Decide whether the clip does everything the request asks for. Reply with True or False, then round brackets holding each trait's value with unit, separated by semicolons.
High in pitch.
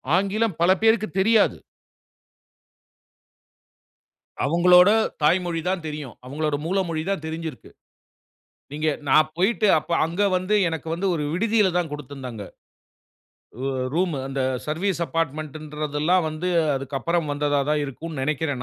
False (160 Hz)